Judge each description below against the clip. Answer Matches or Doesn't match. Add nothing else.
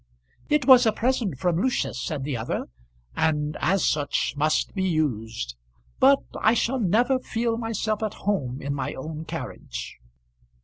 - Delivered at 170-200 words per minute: Doesn't match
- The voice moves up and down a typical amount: Doesn't match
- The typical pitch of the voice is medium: Matches